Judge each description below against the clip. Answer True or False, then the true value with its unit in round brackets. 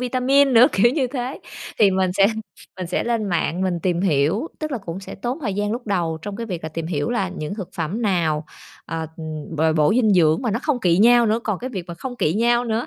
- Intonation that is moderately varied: False (5.8 semitones)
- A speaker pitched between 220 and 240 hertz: False (200 Hz)